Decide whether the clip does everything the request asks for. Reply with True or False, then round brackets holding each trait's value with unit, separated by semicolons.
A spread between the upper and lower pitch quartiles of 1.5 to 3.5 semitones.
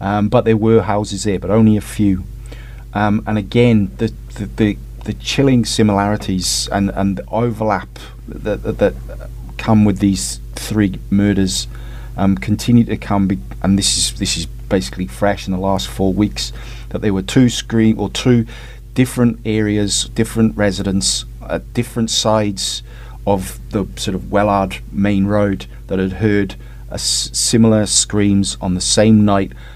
True (2.9 semitones)